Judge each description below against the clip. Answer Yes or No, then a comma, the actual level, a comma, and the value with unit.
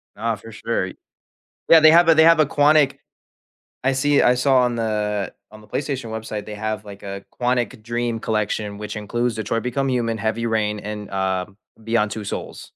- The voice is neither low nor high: No, low, 115 Hz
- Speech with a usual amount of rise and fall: Yes, average, 3.2 semitones